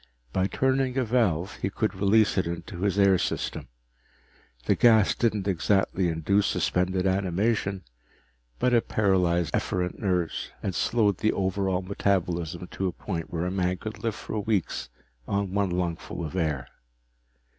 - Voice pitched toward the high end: No, very low, 95 Hz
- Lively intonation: No, narrow, 2.5 semitones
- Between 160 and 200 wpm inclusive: No, average, 150 wpm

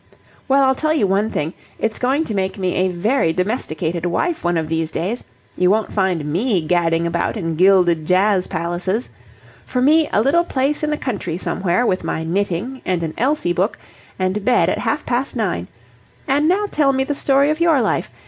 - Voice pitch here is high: Yes, high, 200 Hz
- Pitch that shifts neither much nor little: No, wide, 7.4 semitones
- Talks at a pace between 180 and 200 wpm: Yes, average, 195 wpm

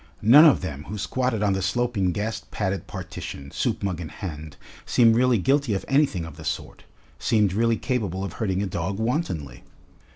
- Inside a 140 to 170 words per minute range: No, average, 185 wpm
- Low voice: Yes, low, 100 Hz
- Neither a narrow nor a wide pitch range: Yes, average, 4.7 semitones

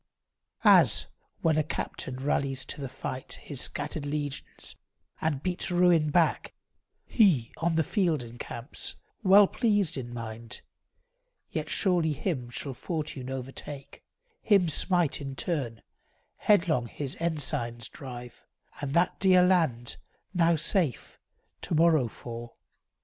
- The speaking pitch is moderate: Yes, medium, 150 Hz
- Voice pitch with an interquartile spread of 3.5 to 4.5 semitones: No, average, 5.0 semitones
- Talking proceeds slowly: Yes, slow, 120 wpm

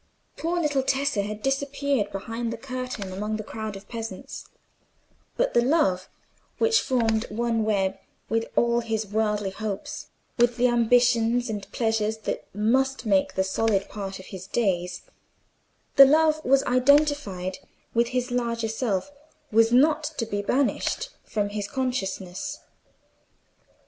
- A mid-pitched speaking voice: No, high, 230 Hz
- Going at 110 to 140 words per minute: Yes, slow, 135 wpm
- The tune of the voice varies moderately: Yes, average, 4.2 semitones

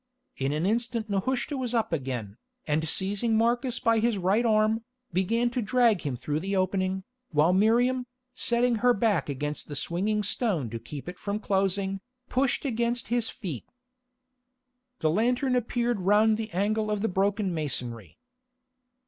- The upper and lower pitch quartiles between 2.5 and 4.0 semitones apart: No, average, 4.9 semitones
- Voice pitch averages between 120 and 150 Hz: No, high, 210 Hz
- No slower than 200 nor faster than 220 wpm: No, average, 155 wpm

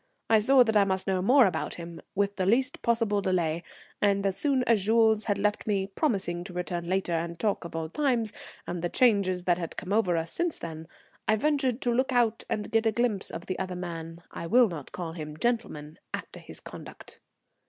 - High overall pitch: Yes, high, 195 Hz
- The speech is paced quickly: Yes, fast, 215 wpm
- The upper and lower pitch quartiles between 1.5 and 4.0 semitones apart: No, average, 4.9 semitones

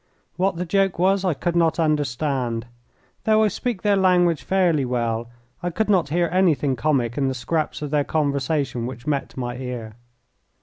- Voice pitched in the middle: Yes, medium, 150 Hz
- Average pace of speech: Yes, average, 175 wpm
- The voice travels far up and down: Yes, wide, 5.7 semitones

